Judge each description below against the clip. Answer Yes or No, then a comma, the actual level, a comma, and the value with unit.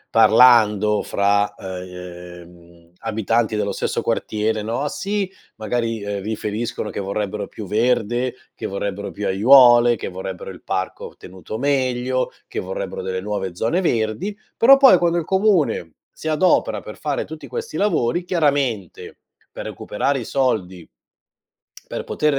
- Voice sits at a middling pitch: No, low, 110 Hz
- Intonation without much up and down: No, wide, 5.4 semitones